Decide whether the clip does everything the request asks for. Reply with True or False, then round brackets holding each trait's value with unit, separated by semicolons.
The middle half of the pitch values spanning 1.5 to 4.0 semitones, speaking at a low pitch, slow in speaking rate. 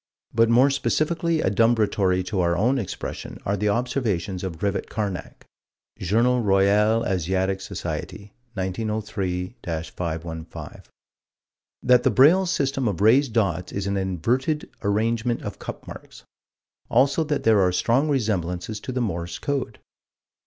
False (5.0 semitones; 105 Hz; 130 wpm)